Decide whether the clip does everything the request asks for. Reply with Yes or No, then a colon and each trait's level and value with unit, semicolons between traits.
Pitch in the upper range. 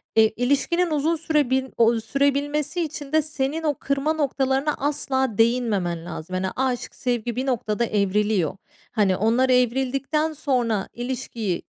Yes: very high, 260 Hz